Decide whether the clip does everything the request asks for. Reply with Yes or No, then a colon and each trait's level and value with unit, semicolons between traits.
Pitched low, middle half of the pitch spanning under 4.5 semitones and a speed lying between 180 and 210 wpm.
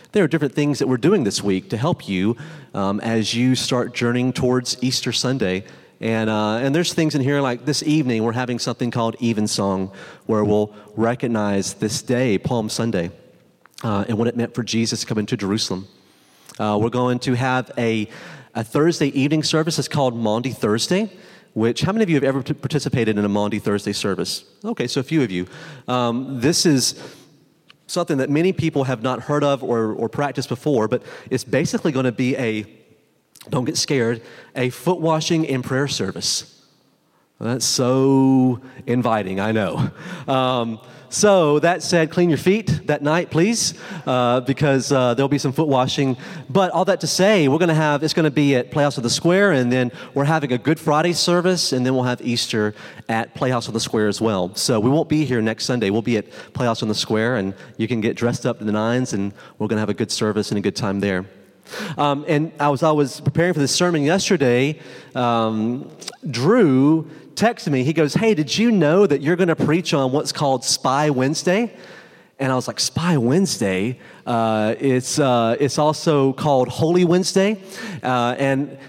No: low, 130 Hz; average, 5.0 semitones; average, 200 wpm